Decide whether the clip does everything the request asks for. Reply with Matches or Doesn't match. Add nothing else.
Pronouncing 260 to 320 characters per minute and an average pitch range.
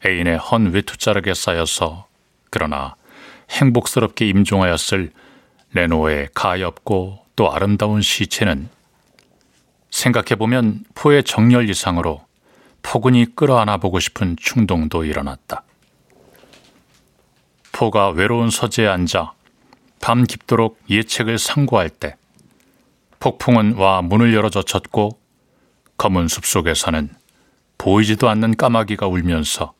Doesn't match